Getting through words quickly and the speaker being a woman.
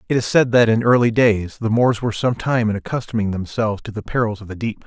No: fast, 260 wpm; male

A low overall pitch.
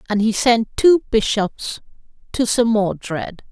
No: high, 220 Hz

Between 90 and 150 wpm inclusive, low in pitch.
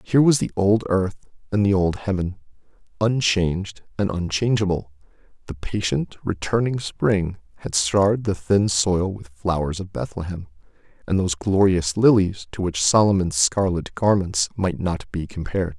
Yes: average, 145 wpm; very low, 95 Hz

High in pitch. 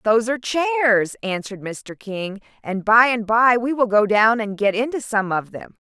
Yes: high, 225 Hz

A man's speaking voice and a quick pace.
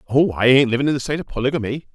Yes: male; fast, 275 wpm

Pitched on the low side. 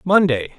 No: medium, 160 Hz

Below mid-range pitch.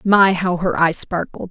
No: medium, 180 Hz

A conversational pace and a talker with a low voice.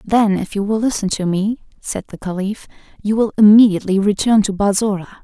No: average, 185 wpm; high, 205 Hz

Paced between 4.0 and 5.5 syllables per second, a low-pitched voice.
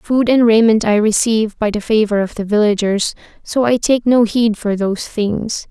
No: 4.8 syllables/s; high, 220 Hz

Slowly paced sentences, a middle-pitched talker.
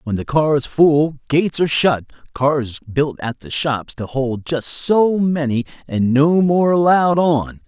No: average, 170 wpm; medium, 145 Hz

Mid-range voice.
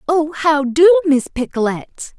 No: very high, 305 Hz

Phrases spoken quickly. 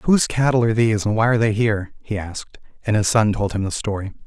Yes: fast, 255 wpm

